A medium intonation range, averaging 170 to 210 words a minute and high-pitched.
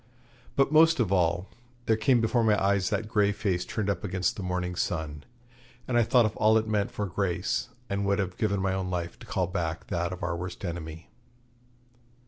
No: average, 3.5 semitones; fast, 205 wpm; low, 100 Hz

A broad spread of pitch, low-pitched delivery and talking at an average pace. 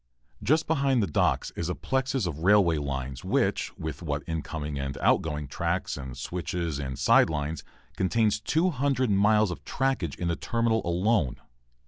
Yes: wide, 7.8 semitones; very low, 90 Hz; average, 155 wpm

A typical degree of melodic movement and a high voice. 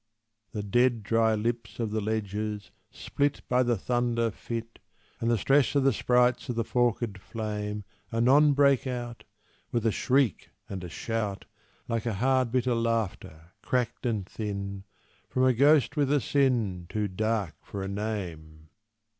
No: average, 3.2 semitones; low, 115 Hz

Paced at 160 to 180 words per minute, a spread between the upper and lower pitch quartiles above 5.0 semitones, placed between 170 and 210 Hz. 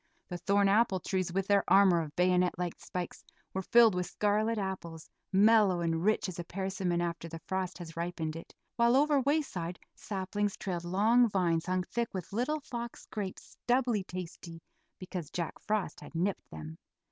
No: average, 170 wpm; average, 3.4 semitones; high, 190 Hz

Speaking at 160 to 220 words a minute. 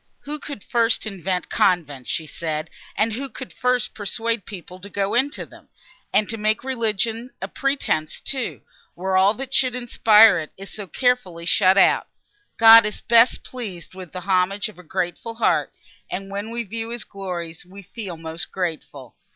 Yes: average, 175 wpm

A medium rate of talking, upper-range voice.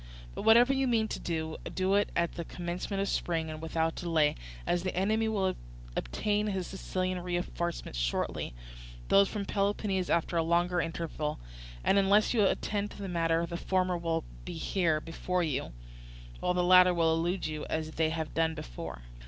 No: average, 175 wpm; medium, 175 Hz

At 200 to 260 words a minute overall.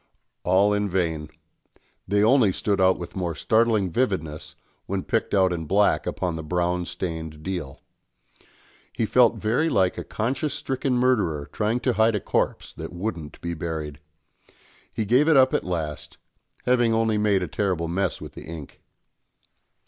No: average, 160 wpm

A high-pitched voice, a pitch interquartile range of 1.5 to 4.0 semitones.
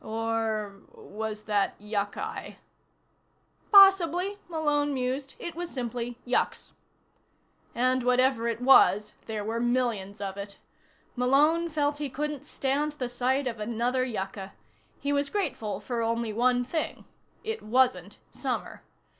No: high, 245 Hz; average, 4.8 semitones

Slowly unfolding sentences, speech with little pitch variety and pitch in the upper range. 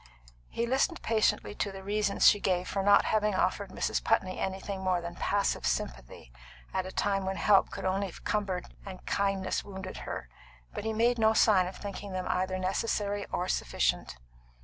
No: average, 180 wpm; narrow, 1.8 semitones; high, 195 Hz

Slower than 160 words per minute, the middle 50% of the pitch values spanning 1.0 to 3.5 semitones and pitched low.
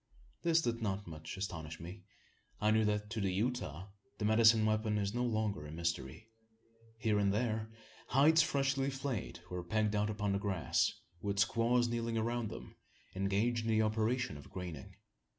No: average, 170 wpm; average, 3.0 semitones; low, 110 Hz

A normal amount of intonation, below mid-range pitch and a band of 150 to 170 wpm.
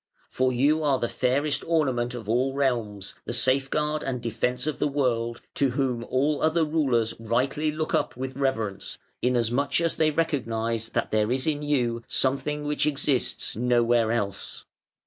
Yes: average, 3.7 semitones; low, 130 Hz; average, 160 wpm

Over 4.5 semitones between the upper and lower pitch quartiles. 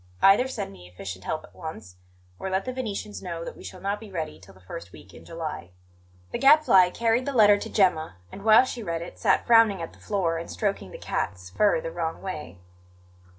Yes: average, 5.2 semitones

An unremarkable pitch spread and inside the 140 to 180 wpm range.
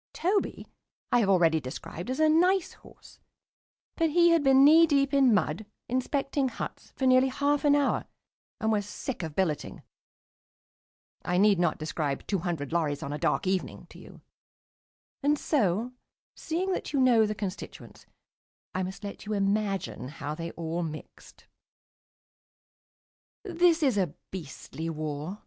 No: wide, 9.0 semitones; average, 150 wpm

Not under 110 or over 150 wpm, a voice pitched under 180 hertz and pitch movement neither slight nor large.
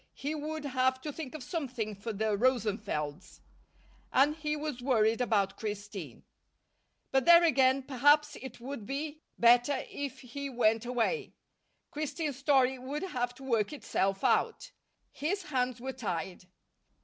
No: average, 140 wpm; very high, 260 Hz; average, 4.5 semitones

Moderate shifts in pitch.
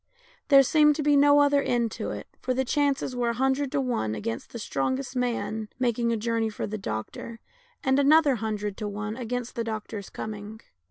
Yes: average, 3.9 semitones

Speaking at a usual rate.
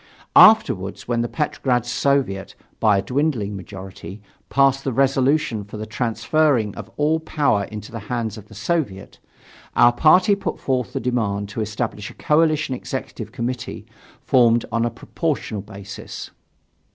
Yes: average, 145 wpm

